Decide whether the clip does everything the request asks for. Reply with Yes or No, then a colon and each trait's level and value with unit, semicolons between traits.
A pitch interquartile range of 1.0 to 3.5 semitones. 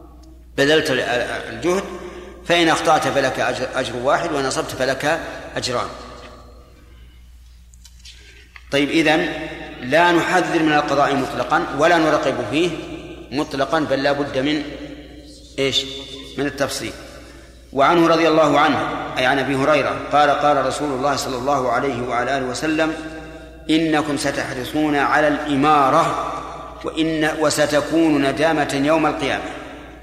Yes: average, 2.8 semitones